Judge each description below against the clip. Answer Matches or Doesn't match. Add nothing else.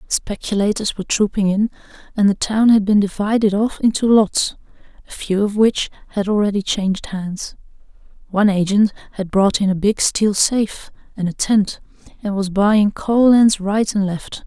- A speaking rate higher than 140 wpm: Matches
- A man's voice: Doesn't match